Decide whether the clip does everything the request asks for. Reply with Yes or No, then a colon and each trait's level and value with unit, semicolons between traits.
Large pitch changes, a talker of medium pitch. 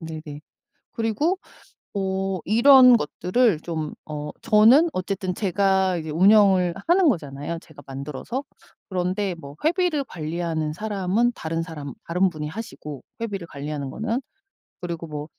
Yes: wide, 5.7 semitones; medium, 180 Hz